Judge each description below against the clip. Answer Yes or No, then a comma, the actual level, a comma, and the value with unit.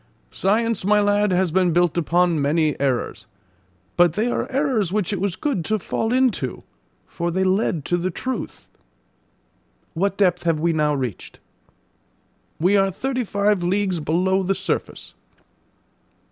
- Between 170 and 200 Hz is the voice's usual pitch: Yes, medium, 185 Hz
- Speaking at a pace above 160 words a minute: No, average, 145 wpm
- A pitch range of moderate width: Yes, average, 3.3 semitones